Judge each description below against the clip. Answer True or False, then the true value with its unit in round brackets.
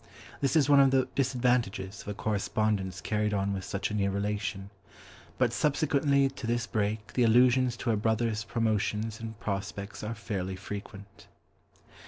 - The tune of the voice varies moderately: True (3.4 semitones)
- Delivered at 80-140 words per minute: False (160 wpm)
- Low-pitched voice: True (110 Hz)